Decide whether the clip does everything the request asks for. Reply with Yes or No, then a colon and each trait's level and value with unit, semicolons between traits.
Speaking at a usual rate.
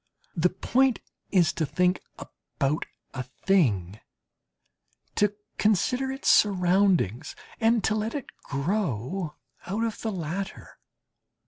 No: slow, 110 wpm